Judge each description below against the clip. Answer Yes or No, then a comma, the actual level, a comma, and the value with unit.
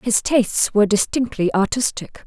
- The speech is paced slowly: Yes, slow, 130 wpm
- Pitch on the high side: Yes, high, 220 Hz